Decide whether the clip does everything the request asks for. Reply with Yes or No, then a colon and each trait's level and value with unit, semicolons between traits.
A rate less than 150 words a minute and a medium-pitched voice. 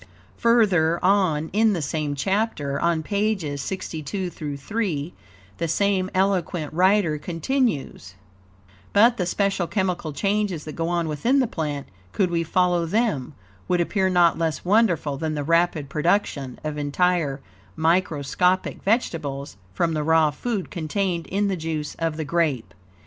Yes: average, 140 wpm; medium, 170 Hz